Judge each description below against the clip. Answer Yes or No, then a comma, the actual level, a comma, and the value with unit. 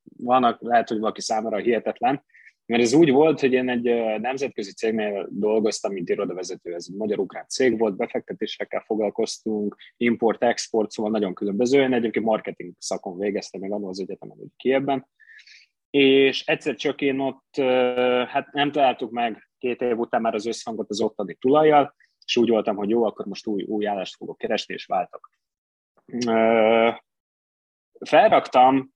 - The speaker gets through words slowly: No, average, 150 wpm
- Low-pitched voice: Yes, low, 115 Hz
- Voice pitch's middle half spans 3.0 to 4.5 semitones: Yes, average, 3.7 semitones